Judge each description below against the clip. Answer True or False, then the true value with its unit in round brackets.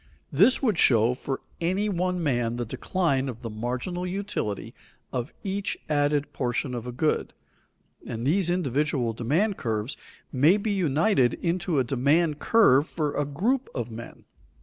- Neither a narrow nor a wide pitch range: False (6.8 semitones)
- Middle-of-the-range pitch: True (145 Hz)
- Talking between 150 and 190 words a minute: True (155 wpm)